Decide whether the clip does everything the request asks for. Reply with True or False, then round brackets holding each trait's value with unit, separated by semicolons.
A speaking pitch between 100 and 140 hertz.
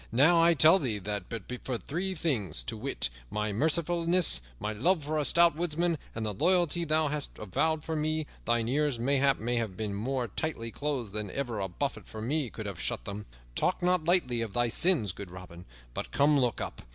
True (135 Hz)